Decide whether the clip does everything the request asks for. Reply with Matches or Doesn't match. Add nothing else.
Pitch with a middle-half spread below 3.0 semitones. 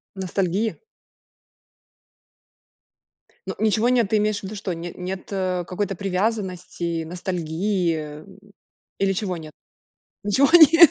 Doesn't match